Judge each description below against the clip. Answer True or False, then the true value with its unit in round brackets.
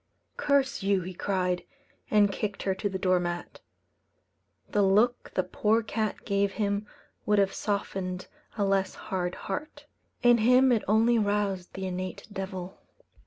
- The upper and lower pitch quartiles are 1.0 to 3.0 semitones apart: True (2.4 semitones)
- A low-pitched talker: False (200 Hz)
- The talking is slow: False (150 wpm)